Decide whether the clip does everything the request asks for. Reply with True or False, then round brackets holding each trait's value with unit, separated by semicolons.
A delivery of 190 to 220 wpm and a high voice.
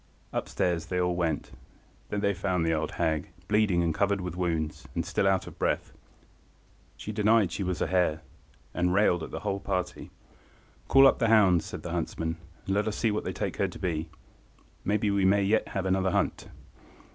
False (195 wpm; 95 Hz)